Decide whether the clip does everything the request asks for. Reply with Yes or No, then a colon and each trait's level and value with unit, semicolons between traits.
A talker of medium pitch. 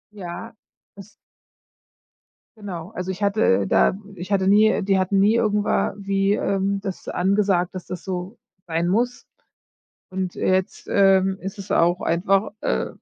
No: high, 195 Hz